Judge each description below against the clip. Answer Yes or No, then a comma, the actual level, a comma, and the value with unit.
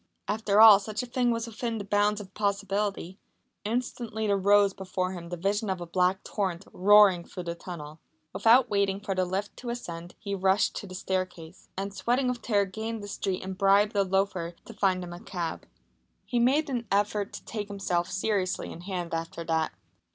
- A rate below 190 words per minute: No, average, 195 wpm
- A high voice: Yes, high, 200 Hz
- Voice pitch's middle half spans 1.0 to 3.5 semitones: Yes, narrow, 2.5 semitones